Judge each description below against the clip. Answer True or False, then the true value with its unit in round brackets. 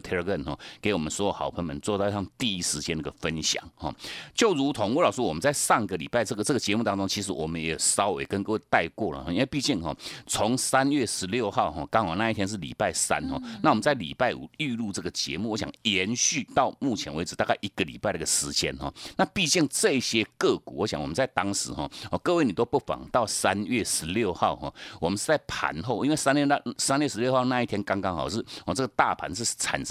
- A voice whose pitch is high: False (105 Hz)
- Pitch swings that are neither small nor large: False (6.0 semitones)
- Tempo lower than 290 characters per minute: False (355 characters per minute)